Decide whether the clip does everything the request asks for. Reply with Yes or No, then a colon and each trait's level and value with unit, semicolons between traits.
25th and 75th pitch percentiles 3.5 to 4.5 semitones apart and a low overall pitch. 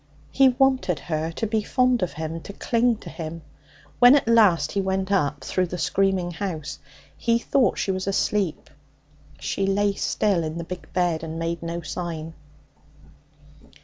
No: average, 4.2 semitones; medium, 185 Hz